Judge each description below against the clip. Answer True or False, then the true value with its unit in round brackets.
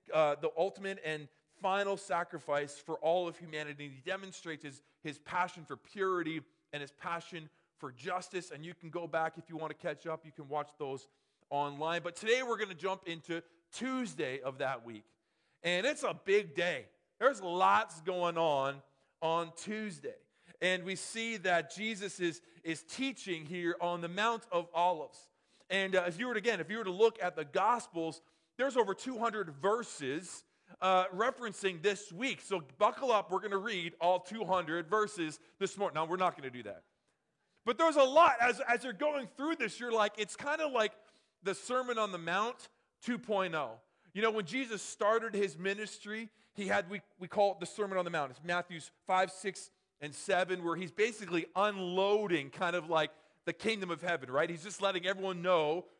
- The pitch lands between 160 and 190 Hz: True (185 Hz)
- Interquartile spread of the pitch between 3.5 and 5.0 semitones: True (4.4 semitones)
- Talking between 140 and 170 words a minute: False (190 wpm)